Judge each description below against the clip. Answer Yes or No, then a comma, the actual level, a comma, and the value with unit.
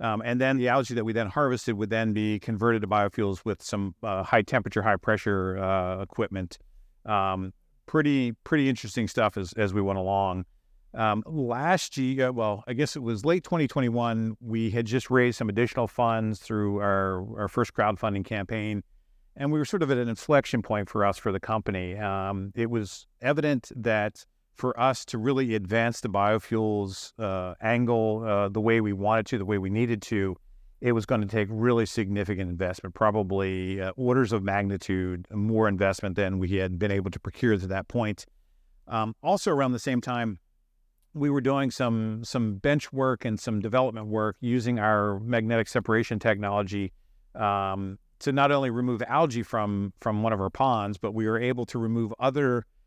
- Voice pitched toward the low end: Yes, low, 110 Hz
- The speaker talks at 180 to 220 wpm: Yes, average, 185 wpm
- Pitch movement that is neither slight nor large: Yes, average, 3.3 semitones